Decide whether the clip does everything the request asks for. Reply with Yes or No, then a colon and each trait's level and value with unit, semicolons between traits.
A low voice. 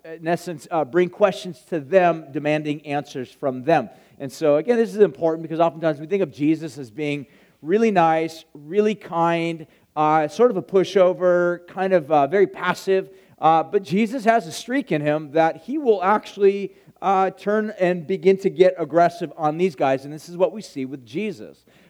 No: medium, 170 Hz